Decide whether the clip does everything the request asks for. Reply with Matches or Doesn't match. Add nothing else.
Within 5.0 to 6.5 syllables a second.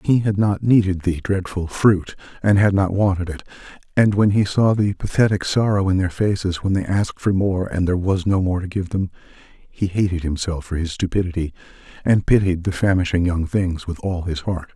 Matches